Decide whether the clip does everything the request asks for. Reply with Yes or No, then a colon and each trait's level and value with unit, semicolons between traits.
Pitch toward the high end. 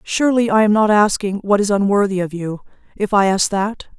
Yes: high, 205 Hz